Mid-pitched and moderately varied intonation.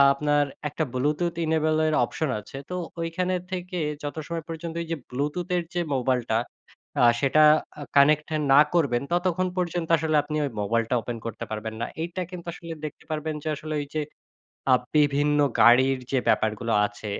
Yes: medium, 150 Hz; average, 4.2 semitones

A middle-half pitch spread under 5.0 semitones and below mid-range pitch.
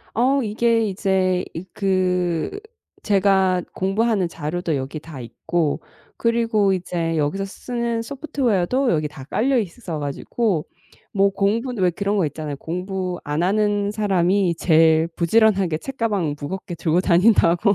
No: average, 4.3 semitones; high, 190 Hz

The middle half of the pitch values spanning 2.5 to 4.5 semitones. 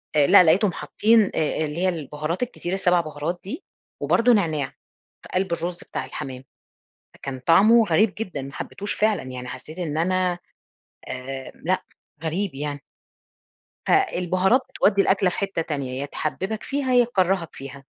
No: average, 5.1 semitones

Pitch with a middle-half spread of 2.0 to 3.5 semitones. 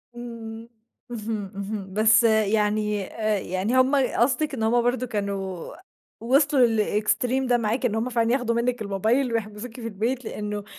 Yes: average, 2.7 semitones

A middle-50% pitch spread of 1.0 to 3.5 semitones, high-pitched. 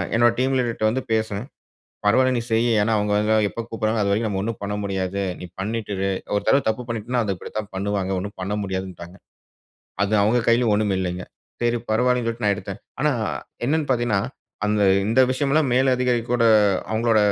No: average, 3.0 semitones; low, 110 Hz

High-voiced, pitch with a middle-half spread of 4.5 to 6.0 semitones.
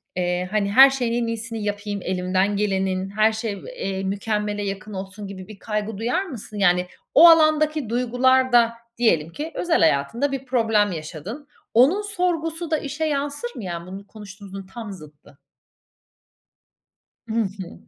Yes: high, 215 Hz; average, 5.3 semitones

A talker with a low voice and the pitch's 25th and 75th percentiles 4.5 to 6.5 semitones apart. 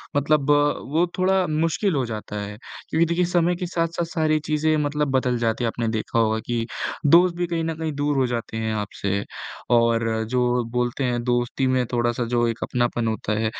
Yes: low, 130 Hz; average, 5.3 semitones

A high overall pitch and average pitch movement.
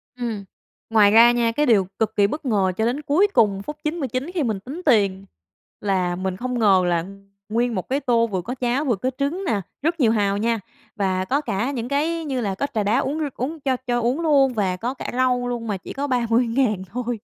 Yes: high, 240 Hz; average, 4.8 semitones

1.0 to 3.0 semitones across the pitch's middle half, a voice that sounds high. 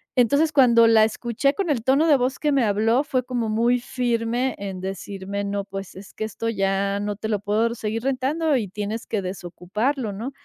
No: average, 4.1 semitones; high, 225 Hz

